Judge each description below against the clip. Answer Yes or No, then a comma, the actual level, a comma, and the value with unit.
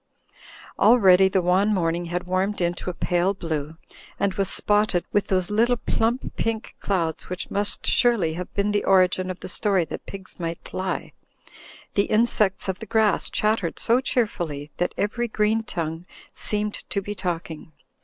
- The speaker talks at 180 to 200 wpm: No, average, 165 wpm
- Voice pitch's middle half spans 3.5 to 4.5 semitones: No, average, 3.1 semitones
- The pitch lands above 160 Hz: Yes, high, 190 Hz